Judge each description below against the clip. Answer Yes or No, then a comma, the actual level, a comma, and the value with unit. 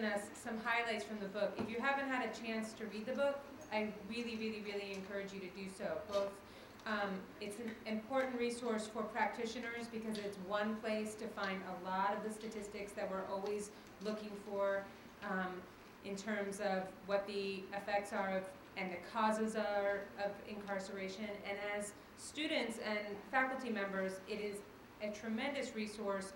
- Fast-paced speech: No, average, 170 wpm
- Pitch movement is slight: Yes, narrow, 1.9 semitones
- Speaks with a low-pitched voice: No, high, 210 Hz